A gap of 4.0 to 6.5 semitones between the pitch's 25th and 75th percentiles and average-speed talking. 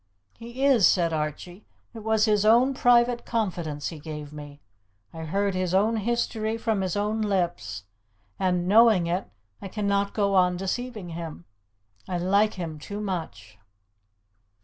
Yes: average, 4.5 semitones; average, 150 wpm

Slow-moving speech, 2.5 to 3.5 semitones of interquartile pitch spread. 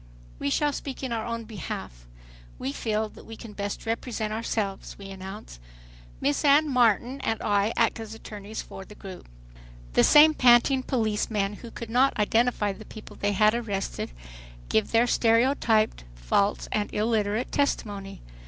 No: average, 155 wpm; average, 2.8 semitones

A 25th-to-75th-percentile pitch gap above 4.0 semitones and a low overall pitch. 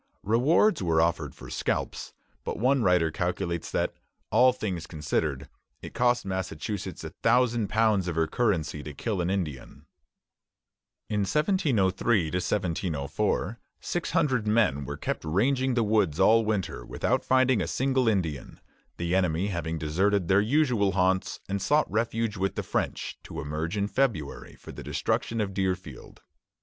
Yes: average, 5.2 semitones; low, 100 Hz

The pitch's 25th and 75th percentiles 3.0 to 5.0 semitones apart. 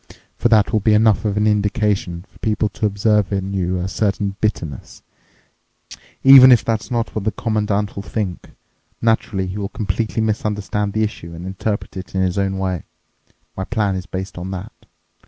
No: narrow, 2.4 semitones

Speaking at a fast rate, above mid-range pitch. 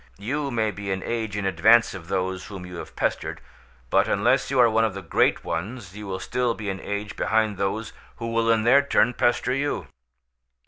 No: fast, 210 wpm; low, 110 Hz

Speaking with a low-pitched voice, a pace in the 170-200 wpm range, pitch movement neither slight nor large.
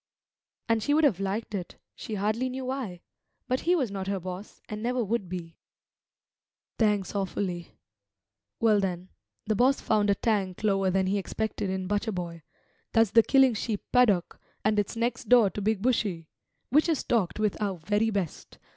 No: high, 210 Hz; average, 175 wpm; average, 3.4 semitones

